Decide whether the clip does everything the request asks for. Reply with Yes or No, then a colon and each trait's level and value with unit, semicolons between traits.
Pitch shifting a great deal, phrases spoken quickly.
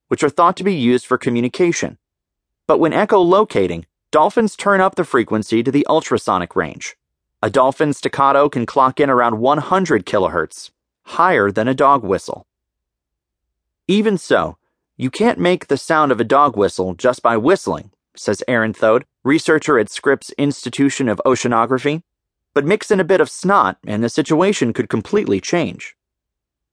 No: wide, 6.5 semitones; average, 155 wpm